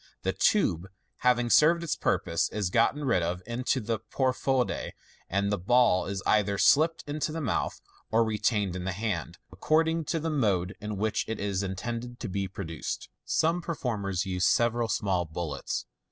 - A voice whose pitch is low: Yes, low, 110 Hz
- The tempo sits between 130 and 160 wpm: No, average, 170 wpm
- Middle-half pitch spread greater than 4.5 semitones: Yes, average, 5.3 semitones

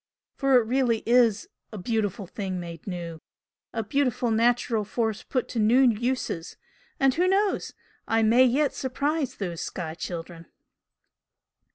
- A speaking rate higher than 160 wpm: No, average, 140 wpm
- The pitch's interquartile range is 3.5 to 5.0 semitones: Yes, average, 4.7 semitones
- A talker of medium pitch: No, high, 230 Hz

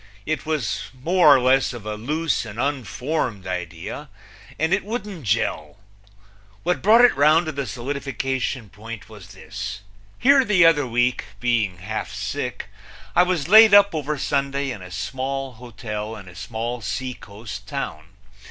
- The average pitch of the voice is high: No, low, 130 Hz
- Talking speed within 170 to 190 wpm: No, average, 150 wpm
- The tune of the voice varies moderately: No, wide, 6.4 semitones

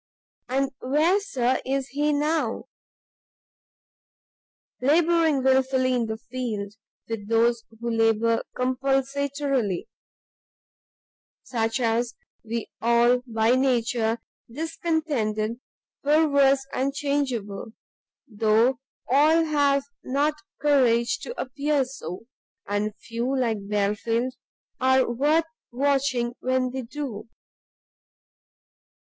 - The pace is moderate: No, slow, 90 wpm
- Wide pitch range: No, average, 3.6 semitones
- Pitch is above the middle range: Yes, very high, 255 Hz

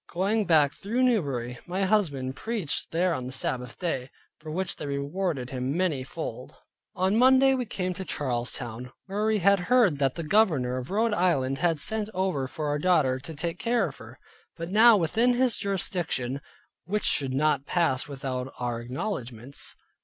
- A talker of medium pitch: Yes, medium, 165 Hz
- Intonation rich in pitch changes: Yes, wide, 7.1 semitones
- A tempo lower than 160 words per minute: No, average, 170 wpm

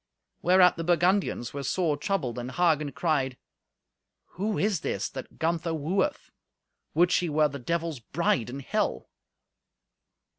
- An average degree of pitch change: Yes, average, 4.3 semitones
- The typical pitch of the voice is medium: Yes, medium, 160 Hz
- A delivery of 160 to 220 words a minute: No, slow, 135 wpm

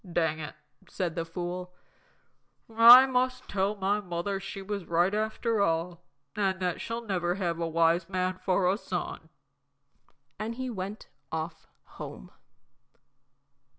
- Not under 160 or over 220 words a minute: No, slow, 135 wpm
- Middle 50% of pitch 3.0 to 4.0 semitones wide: Yes, average, 3.5 semitones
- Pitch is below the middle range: No, medium, 185 Hz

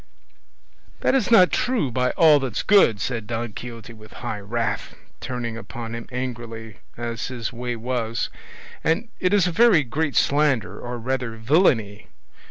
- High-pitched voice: No, low, 120 Hz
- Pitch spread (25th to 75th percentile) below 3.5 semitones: No, average, 4.3 semitones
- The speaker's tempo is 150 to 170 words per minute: Yes, average, 155 wpm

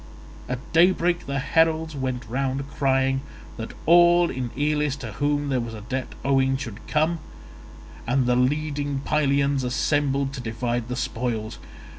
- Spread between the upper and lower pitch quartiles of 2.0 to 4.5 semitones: Yes, average, 2.9 semitones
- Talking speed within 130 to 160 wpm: Yes, average, 145 wpm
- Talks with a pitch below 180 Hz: Yes, low, 135 Hz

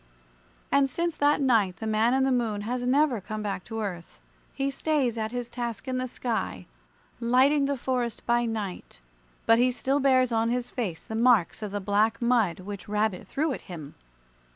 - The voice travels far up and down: No, average, 3.3 semitones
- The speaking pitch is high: Yes, high, 235 Hz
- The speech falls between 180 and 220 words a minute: Yes, average, 190 wpm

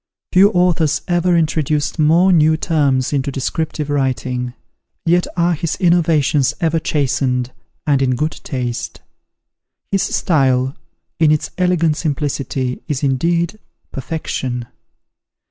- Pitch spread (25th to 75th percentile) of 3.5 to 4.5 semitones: Yes, average, 4.0 semitones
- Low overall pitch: No, medium, 150 Hz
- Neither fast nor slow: No, slow, 110 wpm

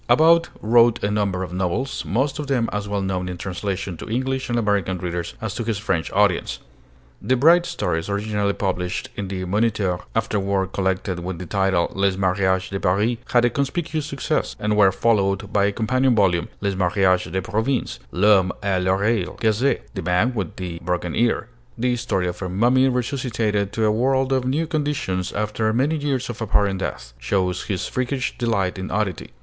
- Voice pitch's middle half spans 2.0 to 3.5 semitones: No, average, 4.4 semitones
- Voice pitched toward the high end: No, low, 105 Hz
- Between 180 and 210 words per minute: Yes, average, 185 wpm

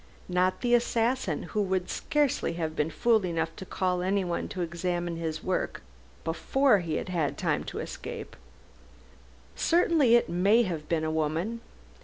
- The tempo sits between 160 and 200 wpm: No, average, 150 wpm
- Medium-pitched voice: Yes, medium, 180 Hz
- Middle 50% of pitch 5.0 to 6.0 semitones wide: Yes, wide, 5.4 semitones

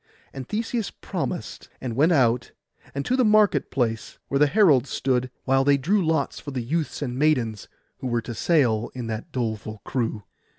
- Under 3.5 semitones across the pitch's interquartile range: No, average, 5.0 semitones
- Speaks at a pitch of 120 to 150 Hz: Yes, low, 135 Hz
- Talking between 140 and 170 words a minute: No, average, 180 wpm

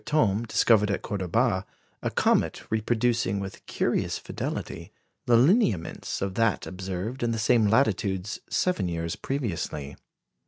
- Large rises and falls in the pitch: No, average, 3.9 semitones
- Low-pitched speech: Yes, low, 105 Hz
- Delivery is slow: Yes, slow, 125 wpm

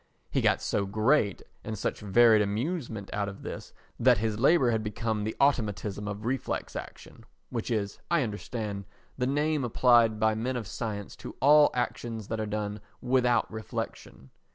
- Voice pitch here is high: No, low, 110 Hz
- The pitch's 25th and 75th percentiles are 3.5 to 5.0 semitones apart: No, average, 3.0 semitones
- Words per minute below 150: No, average, 160 wpm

